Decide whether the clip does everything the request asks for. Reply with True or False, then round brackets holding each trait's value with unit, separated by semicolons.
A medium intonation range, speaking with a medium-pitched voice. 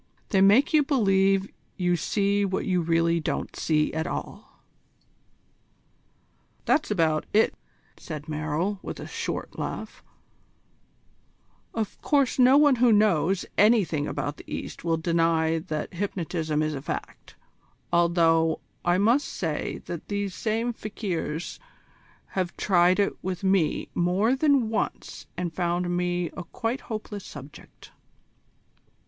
True (4.2 semitones; 180 Hz)